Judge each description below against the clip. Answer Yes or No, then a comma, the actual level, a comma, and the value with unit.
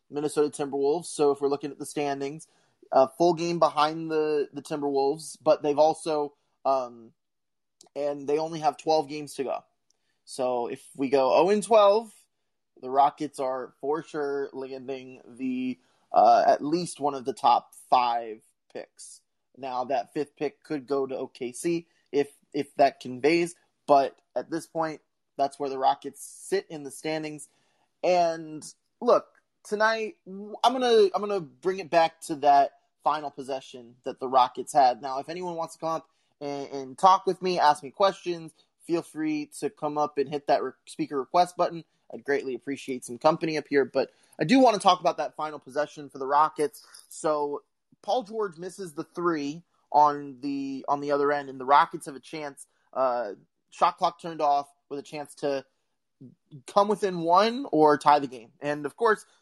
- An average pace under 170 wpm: No, average, 175 wpm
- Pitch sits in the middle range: Yes, medium, 150 Hz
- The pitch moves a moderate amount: Yes, average, 3.6 semitones